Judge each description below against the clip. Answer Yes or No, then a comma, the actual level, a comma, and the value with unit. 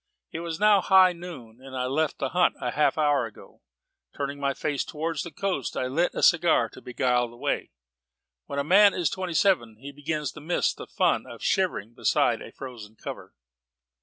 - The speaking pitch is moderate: Yes, medium, 145 Hz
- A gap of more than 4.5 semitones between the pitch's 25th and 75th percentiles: Yes, average, 5.2 semitones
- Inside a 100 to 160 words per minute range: No, average, 200 wpm